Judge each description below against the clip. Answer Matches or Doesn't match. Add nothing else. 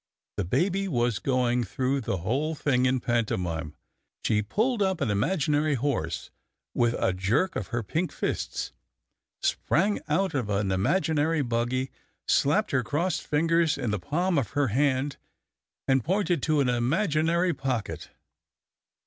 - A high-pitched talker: Doesn't match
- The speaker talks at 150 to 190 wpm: Doesn't match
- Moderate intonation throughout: Doesn't match